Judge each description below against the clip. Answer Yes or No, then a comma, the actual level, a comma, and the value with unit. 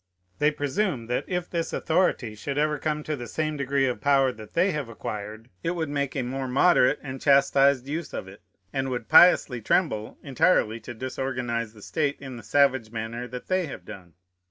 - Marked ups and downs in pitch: No, average, 4.2 semitones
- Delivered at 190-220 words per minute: Yes, average, 195 wpm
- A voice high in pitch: No, low, 135 Hz